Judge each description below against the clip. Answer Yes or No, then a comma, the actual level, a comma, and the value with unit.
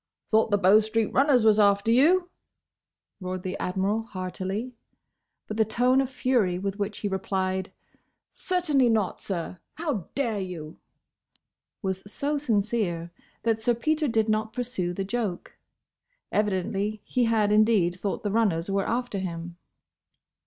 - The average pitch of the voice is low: No, high, 210 Hz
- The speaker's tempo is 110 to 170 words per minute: Yes, average, 140 wpm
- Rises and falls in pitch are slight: No, average, 3.9 semitones